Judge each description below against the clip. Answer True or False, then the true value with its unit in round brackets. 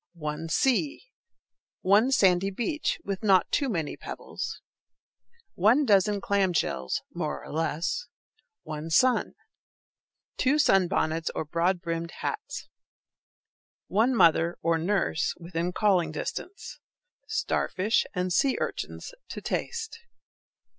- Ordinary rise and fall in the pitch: False (6.3 semitones)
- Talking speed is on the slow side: True (110 wpm)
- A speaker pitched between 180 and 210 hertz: True (190 Hz)